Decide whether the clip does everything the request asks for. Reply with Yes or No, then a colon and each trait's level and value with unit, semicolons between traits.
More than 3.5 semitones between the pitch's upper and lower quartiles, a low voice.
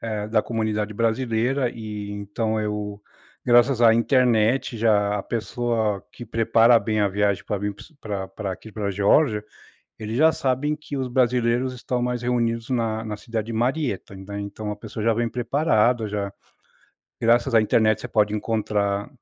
No: narrow, 2.6 semitones; low, 110 Hz